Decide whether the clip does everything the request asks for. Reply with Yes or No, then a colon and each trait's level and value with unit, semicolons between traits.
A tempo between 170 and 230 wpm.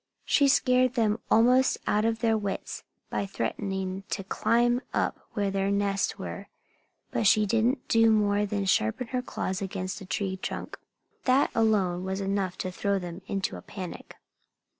No: average, 160 wpm